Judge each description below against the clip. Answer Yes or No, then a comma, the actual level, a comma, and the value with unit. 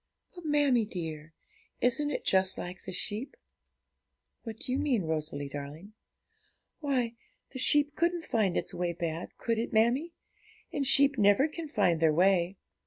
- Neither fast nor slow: Yes, average, 150 wpm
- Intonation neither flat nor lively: No, wide, 8.2 semitones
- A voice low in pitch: No, high, 220 Hz